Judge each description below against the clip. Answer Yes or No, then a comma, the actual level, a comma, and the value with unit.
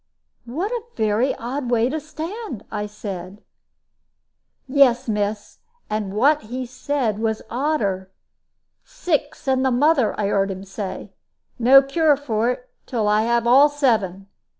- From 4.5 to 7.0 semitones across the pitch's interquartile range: Yes, average, 5.3 semitones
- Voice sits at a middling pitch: No, high, 240 Hz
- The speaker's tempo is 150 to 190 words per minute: No, average, 140 wpm